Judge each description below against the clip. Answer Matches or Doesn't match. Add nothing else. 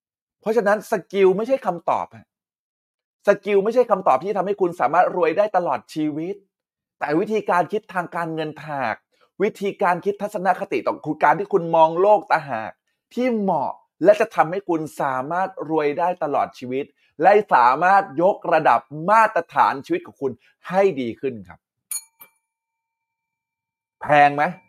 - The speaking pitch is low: Doesn't match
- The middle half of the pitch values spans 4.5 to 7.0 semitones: Matches